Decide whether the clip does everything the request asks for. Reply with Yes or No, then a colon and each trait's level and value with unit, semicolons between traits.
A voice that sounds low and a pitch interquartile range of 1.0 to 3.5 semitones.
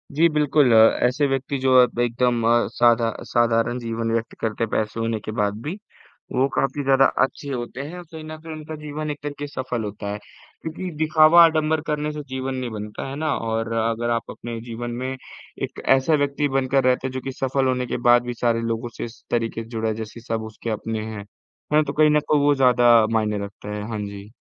No: low, 125 Hz; average, 4.1 semitones